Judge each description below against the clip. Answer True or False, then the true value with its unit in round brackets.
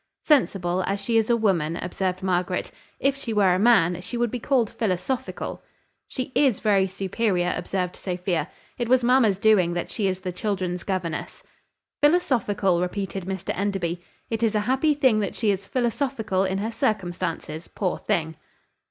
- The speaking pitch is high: True (195 Hz)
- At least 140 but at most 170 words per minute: True (165 wpm)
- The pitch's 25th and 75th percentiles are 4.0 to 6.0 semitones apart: True (4.3 semitones)